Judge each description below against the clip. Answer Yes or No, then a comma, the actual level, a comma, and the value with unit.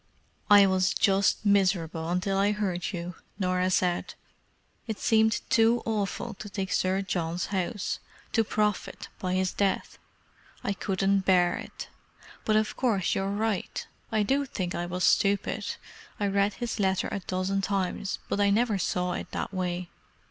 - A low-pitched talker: No, high, 195 Hz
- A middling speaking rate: Yes, average, 150 wpm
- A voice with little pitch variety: Yes, narrow, 2.2 semitones